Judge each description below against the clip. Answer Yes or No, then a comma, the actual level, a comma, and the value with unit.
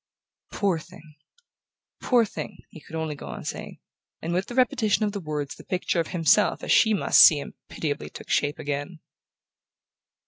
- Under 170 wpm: No, average, 175 wpm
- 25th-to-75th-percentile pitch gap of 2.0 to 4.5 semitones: No, average, 5.1 semitones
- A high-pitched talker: No, medium, 165 Hz